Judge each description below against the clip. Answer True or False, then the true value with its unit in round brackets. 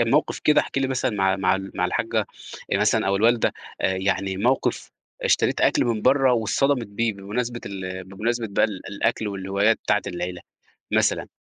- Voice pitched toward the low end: True (105 Hz)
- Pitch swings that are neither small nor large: True (3.7 semitones)